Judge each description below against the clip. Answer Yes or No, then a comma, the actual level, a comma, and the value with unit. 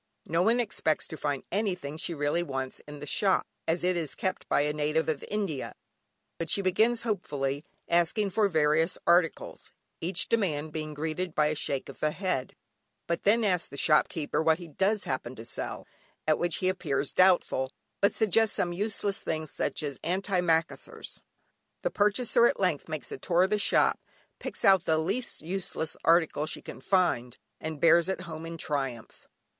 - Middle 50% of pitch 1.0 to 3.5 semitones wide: No, average, 4.0 semitones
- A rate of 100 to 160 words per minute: No, average, 180 wpm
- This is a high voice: No, medium, 165 Hz